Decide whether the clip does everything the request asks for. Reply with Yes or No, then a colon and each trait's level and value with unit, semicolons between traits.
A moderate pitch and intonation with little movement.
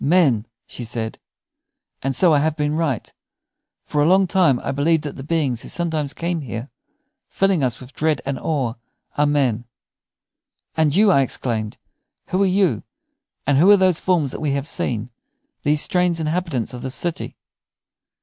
No: medium, 150 Hz; average, 4.5 semitones